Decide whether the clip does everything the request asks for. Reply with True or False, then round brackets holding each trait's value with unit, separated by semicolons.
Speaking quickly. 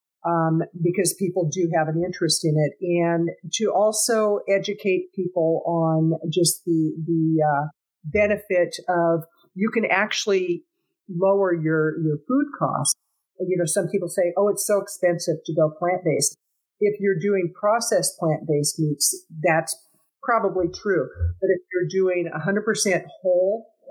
False (150 wpm)